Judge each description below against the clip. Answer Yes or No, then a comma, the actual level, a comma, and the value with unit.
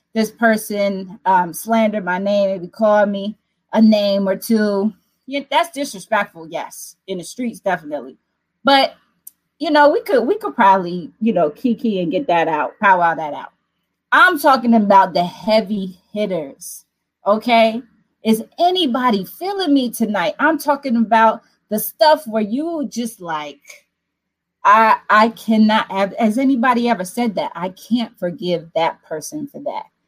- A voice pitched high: Yes, high, 220 Hz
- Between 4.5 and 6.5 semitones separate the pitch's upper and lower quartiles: Yes, average, 5.2 semitones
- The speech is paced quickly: No, average, 150 wpm